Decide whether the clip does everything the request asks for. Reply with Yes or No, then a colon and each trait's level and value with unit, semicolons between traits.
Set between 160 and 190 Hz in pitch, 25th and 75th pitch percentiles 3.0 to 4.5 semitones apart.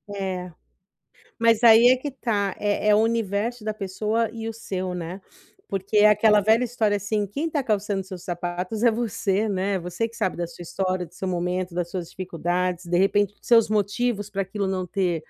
No: high, 200 Hz; average, 3.3 semitones